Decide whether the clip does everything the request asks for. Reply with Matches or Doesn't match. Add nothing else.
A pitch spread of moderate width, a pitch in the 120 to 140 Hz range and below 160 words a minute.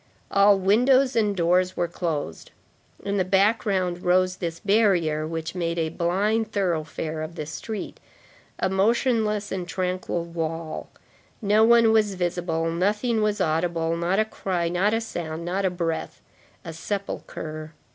Doesn't match